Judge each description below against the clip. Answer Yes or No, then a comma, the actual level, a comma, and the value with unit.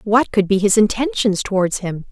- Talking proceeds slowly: No, average, 200 wpm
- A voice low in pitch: No, high, 210 Hz